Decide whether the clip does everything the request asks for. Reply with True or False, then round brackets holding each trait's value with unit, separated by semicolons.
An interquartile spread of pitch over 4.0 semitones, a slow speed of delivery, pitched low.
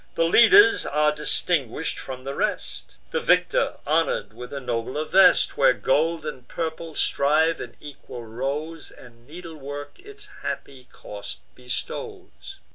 False (4.6 semitones; 130 wpm; 150 Hz)